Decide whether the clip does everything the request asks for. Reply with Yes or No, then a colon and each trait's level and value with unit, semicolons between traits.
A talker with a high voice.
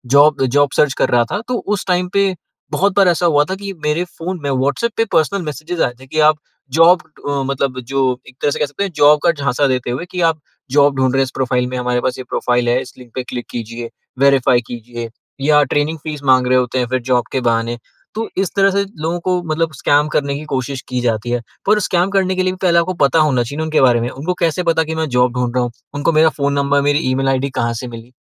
No: medium, 140 Hz